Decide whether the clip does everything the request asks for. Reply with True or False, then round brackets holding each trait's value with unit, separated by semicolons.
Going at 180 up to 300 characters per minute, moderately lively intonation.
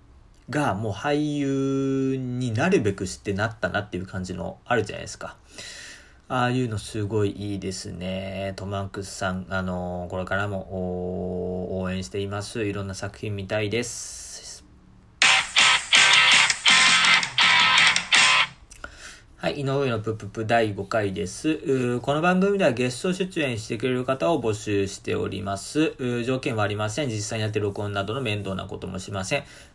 True (295 characters per minute; 4.8 semitones)